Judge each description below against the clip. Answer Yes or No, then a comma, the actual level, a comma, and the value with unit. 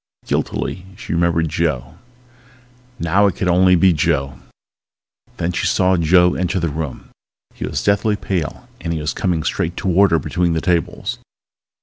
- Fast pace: No, average, 155 wpm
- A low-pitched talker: Yes, very low, 85 Hz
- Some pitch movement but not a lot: No, narrow, 2.2 semitones